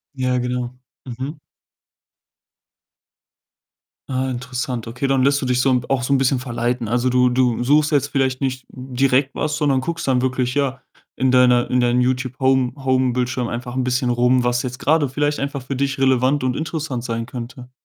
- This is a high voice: No, low, 130 Hz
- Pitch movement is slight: Yes, narrow, 1.5 semitones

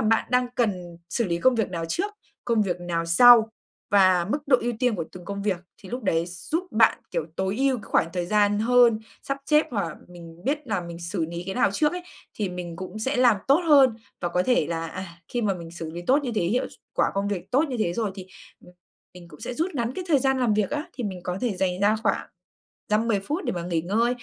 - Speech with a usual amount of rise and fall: No, wide, 5.8 semitones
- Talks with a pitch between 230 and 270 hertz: No, high, 205 Hz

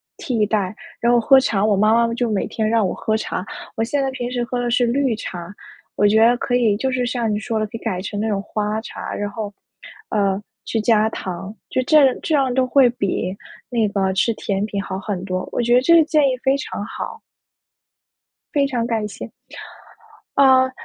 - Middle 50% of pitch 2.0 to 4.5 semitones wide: Yes, average, 3.5 semitones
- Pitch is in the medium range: No, high, 225 Hz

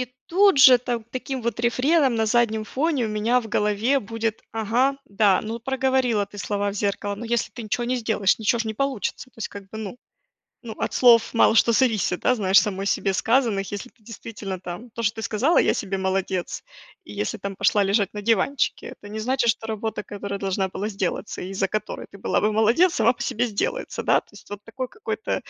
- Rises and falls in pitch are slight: No, average, 3.3 semitones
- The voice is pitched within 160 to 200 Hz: No, high, 220 Hz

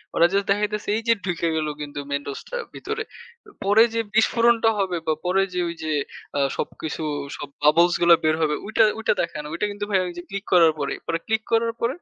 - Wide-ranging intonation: Yes, wide, 5.7 semitones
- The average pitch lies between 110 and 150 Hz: No, medium, 185 Hz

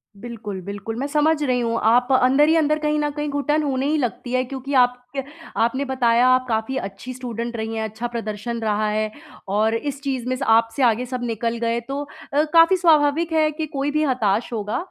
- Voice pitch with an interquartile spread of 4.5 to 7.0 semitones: No, average, 4.1 semitones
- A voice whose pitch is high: Yes, very high, 250 Hz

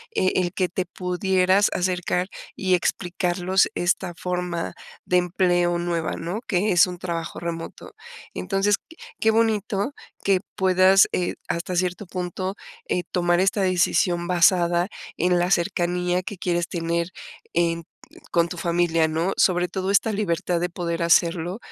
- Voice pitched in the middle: Yes, medium, 180 Hz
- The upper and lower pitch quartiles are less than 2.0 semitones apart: Yes, narrow, 1.5 semitones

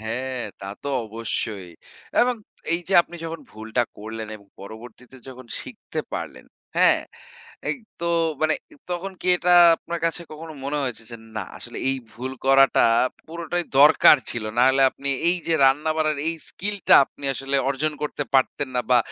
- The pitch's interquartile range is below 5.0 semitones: No, wide, 5.5 semitones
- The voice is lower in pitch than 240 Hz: Yes, low, 135 Hz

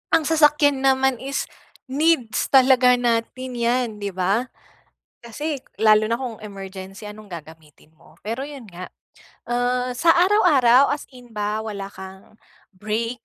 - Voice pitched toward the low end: No, high, 240 Hz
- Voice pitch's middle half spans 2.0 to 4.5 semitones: Yes, average, 4.2 semitones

